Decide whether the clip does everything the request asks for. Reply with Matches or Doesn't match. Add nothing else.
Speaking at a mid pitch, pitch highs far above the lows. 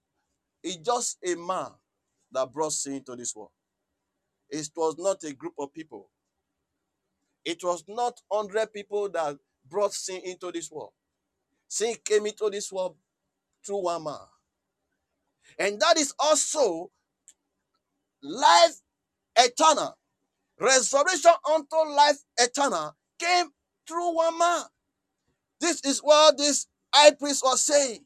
Doesn't match